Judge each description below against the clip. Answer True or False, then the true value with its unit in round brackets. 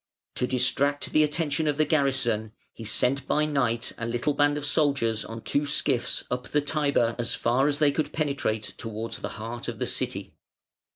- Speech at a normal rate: True (185 wpm)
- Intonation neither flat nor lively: True (4.0 semitones)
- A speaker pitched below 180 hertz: True (140 Hz)